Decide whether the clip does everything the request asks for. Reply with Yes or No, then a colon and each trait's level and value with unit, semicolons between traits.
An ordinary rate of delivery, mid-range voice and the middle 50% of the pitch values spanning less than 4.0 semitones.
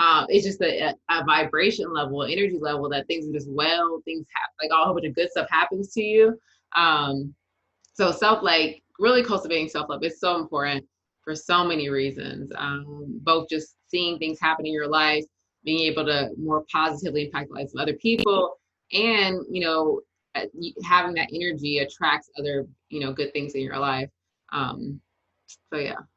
Yes: average, 180 wpm; medium, 155 Hz; average, 3.4 semitones